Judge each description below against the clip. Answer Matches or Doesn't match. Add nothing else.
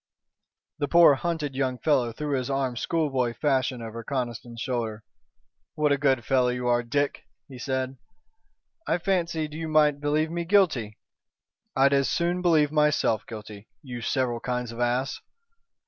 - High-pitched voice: Doesn't match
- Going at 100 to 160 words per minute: Matches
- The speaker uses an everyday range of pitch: Matches